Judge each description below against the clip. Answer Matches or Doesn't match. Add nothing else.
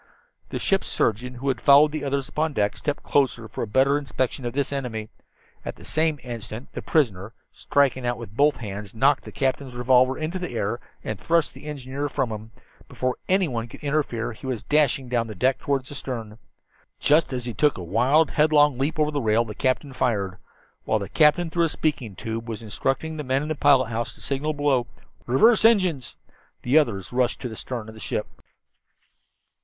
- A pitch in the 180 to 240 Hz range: Doesn't match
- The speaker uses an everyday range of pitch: Matches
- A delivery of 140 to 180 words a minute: Doesn't match